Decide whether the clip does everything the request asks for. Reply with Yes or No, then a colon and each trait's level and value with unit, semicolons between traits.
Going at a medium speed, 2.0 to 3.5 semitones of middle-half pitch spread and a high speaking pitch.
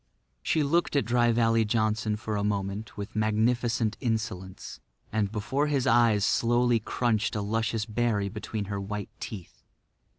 No: average, 145 wpm; narrow, 2.5 semitones; low, 110 Hz